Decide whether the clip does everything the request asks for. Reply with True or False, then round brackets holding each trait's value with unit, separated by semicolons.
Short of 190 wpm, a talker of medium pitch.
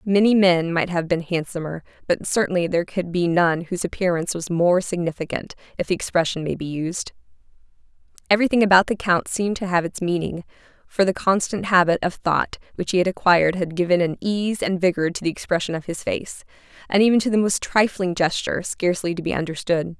False (195 wpm; 180 Hz)